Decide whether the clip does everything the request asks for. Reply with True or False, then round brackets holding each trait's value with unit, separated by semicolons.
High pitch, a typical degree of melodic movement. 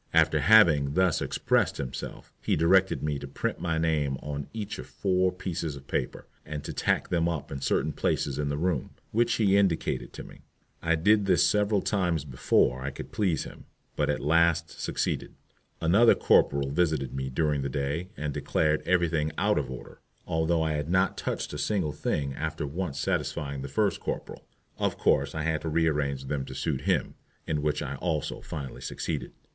False (80 Hz; 3.9 semitones)